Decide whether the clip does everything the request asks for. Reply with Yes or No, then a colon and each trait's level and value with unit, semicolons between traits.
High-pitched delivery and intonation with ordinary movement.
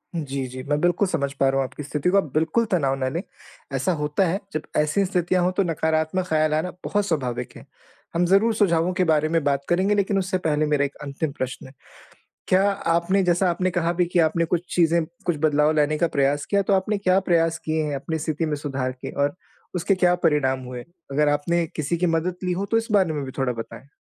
No: medium, 165 Hz; average, 3.8 semitones